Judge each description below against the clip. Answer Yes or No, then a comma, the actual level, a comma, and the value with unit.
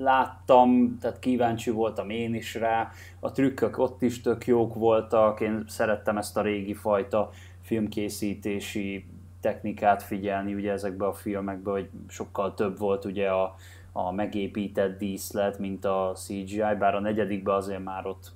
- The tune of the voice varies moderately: No, narrow, 2.0 semitones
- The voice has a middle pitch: No, low, 100 Hz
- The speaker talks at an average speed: Yes, average, 145 wpm